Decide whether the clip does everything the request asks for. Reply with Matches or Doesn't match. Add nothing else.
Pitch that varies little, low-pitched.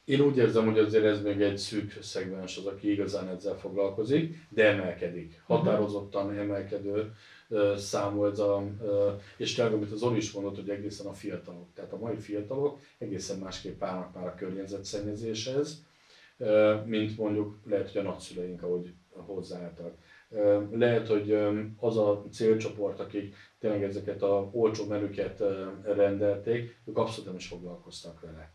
Matches